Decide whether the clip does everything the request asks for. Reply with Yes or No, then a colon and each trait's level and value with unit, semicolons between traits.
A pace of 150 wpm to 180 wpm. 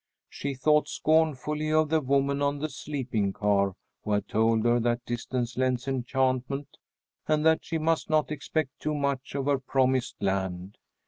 Yes: average, 160 wpm